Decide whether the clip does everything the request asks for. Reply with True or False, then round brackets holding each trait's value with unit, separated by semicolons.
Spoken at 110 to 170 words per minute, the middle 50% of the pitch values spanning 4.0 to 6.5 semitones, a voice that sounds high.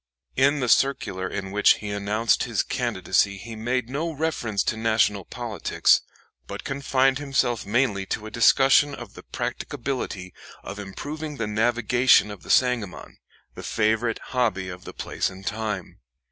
False (150 wpm; 4.3 semitones; 115 Hz)